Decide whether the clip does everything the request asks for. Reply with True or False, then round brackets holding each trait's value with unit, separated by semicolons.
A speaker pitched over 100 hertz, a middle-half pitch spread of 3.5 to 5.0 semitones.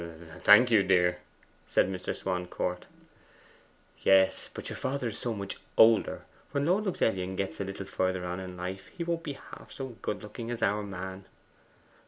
False (95 Hz; 4.1 semitones)